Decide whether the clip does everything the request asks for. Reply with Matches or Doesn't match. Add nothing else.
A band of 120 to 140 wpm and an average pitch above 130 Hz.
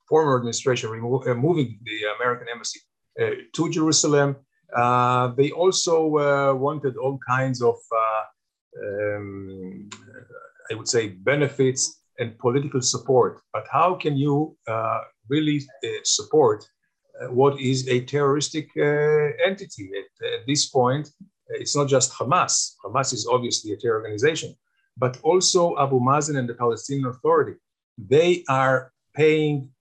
Matches